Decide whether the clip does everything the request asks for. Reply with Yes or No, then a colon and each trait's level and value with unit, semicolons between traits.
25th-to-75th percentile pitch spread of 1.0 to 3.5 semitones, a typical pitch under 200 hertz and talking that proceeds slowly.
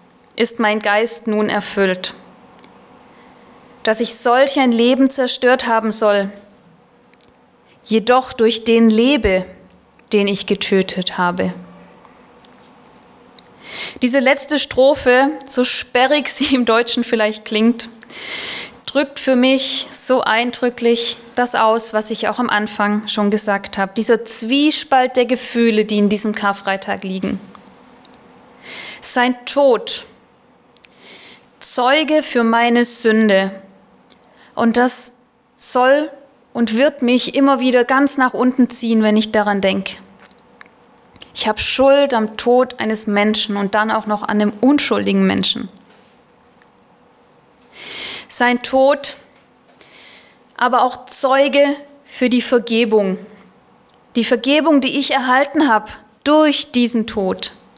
No: average, 3.2 semitones; high, 235 Hz; slow, 115 wpm